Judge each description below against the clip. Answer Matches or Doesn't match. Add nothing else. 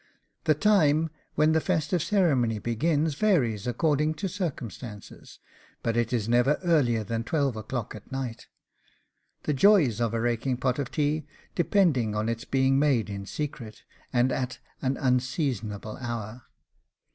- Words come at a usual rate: Matches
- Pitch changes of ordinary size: Matches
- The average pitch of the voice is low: Matches